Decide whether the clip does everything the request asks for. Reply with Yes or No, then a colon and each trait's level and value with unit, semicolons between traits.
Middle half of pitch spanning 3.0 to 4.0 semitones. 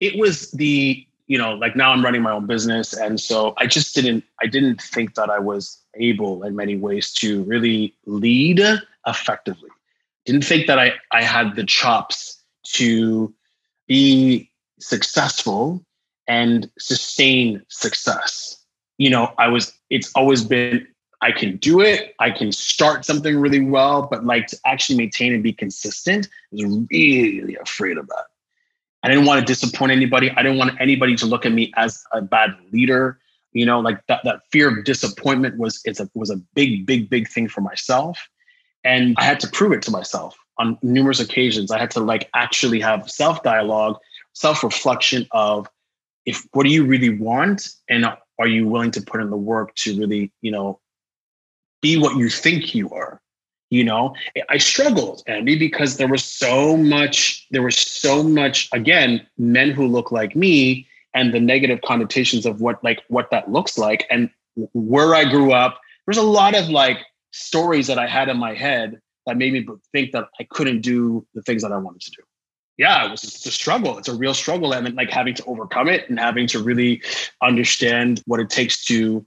Yes: average, 3.4 semitones